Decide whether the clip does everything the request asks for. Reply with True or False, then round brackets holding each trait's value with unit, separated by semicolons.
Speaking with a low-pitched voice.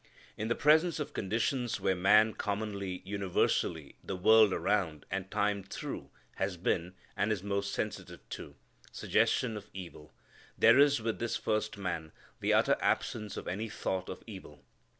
True (100 Hz)